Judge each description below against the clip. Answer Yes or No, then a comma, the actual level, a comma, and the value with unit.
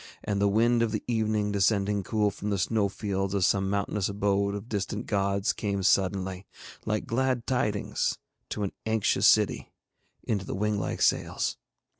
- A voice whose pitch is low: Yes, low, 100 Hz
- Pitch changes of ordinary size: No, narrow, 1.5 semitones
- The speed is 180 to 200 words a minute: No, average, 160 wpm